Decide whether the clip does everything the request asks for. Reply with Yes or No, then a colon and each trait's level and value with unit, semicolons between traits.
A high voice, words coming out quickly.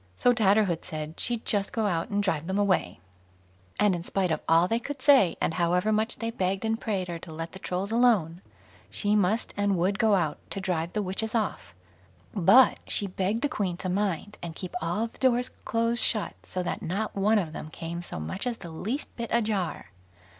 Yes: high, 195 Hz; fast, 210 wpm